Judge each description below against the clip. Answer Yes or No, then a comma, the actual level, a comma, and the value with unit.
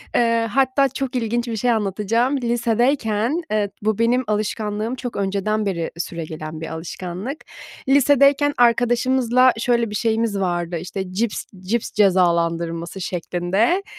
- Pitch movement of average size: Yes, average, 4.5 semitones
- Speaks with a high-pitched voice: Yes, high, 220 Hz